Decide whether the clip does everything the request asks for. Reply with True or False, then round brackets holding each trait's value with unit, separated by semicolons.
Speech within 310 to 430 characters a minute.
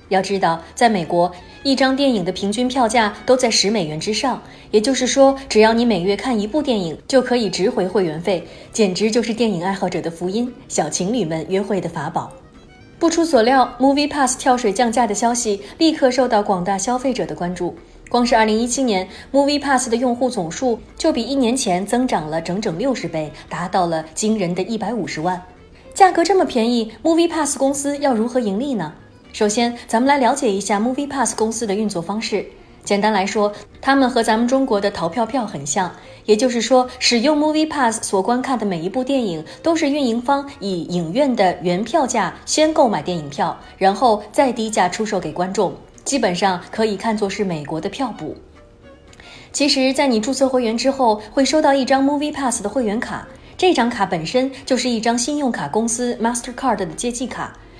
True (335 characters per minute)